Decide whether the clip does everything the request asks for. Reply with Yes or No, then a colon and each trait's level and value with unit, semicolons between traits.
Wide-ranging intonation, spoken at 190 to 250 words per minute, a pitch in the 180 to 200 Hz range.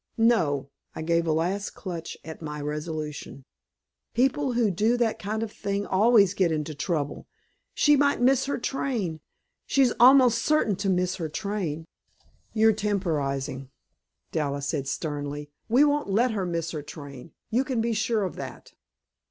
No: wide, 7.0 semitones; average, 155 wpm; high, 190 Hz